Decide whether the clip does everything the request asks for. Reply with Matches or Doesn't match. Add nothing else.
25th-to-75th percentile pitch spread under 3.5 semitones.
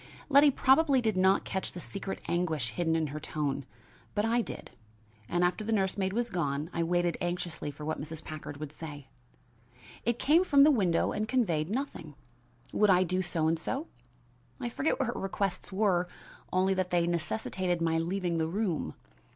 Doesn't match